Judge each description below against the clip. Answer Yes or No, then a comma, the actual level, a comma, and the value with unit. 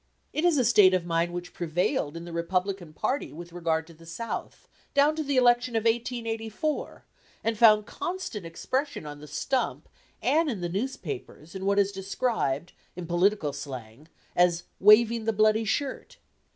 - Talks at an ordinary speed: Yes, average, 165 wpm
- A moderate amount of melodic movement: No, wide, 5.9 semitones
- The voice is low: No, high, 200 Hz